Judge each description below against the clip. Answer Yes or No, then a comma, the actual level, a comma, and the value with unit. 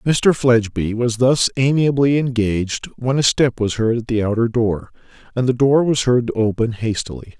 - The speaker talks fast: No, average, 185 wpm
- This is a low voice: Yes, low, 120 Hz